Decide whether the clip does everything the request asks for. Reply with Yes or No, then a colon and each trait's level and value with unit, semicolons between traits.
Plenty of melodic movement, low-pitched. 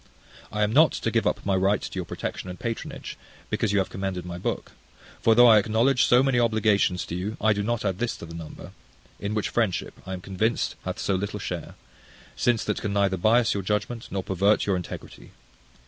No: average, 3.0 semitones; low, 105 Hz